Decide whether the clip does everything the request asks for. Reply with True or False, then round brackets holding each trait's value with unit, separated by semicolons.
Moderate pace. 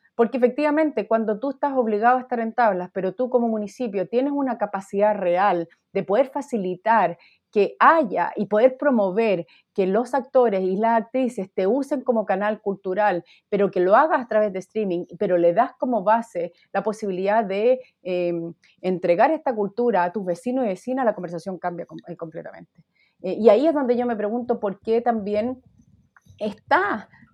True (170 wpm)